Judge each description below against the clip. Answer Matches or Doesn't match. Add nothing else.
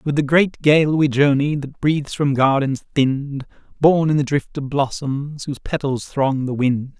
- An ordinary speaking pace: Matches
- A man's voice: Matches